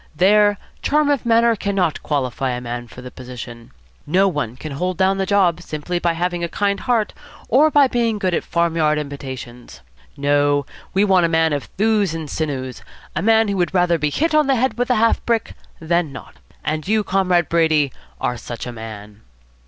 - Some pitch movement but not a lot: No, wide, 6.2 semitones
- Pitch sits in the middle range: Yes, medium, 170 Hz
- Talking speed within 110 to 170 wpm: No, average, 190 wpm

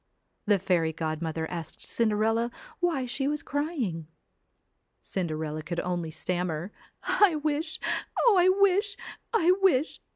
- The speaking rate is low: Yes, slow, 120 wpm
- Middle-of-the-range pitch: No, high, 225 Hz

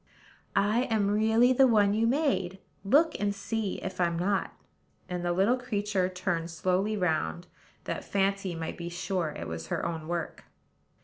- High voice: Yes, high, 195 Hz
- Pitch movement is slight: No, average, 3.8 semitones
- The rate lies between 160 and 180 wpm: Yes, average, 165 wpm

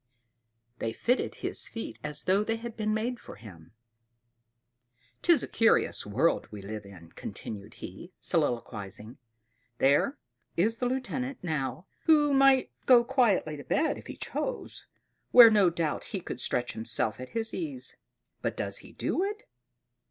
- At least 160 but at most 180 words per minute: No, average, 150 wpm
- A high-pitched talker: Yes, high, 195 Hz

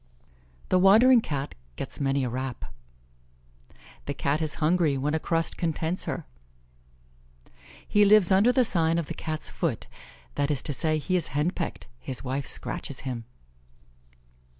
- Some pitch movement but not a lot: Yes, average, 4.6 semitones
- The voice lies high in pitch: No, medium, 155 Hz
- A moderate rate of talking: Yes, average, 150 wpm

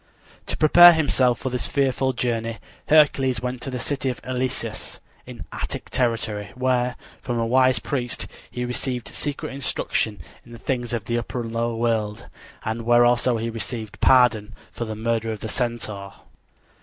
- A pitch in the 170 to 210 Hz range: No, low, 120 Hz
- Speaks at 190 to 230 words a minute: No, average, 170 wpm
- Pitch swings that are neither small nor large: No, narrow, 2.1 semitones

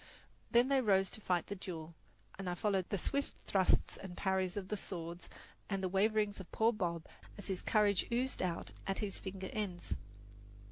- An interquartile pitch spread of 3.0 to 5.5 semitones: No, narrow, 2.6 semitones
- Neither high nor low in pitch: No, high, 195 Hz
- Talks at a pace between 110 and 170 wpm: No, average, 185 wpm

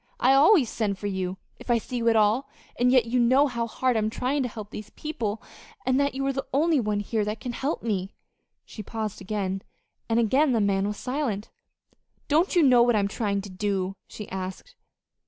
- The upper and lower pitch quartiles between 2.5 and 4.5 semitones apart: Yes, average, 4.1 semitones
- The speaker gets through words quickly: Yes, fast, 210 wpm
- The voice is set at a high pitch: Yes, high, 230 Hz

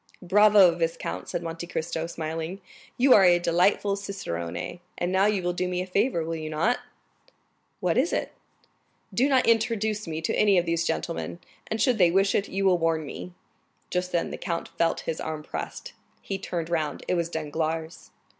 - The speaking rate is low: No, average, 185 wpm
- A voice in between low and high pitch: Yes, medium, 175 Hz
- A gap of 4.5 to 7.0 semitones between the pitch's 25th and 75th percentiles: No, average, 3.4 semitones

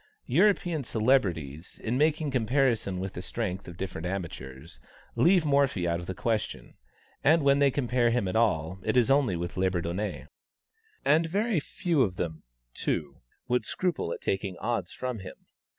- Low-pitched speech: Yes, low, 115 Hz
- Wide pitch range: Yes, wide, 7.5 semitones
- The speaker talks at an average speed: Yes, average, 160 wpm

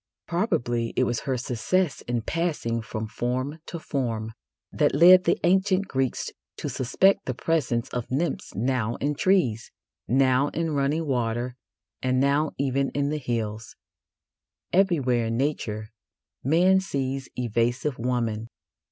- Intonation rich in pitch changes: No, average, 4.6 semitones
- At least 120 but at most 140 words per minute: Yes, slow, 135 wpm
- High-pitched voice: No, low, 130 Hz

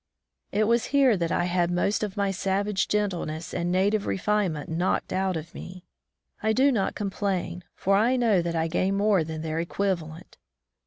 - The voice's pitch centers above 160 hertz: Yes, high, 190 Hz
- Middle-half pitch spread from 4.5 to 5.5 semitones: No, average, 3.3 semitones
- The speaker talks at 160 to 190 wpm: Yes, average, 175 wpm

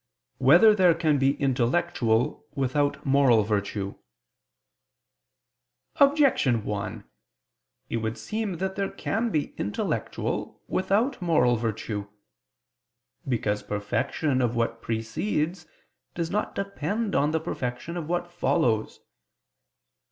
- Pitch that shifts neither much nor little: No, wide, 7.4 semitones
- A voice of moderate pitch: Yes, medium, 145 Hz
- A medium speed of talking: No, slow, 105 wpm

